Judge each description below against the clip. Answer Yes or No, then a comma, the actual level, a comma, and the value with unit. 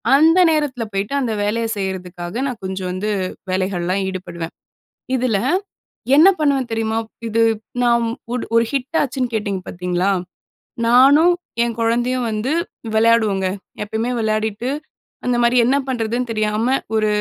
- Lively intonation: No, average, 4.0 semitones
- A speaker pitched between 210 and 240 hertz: Yes, high, 225 Hz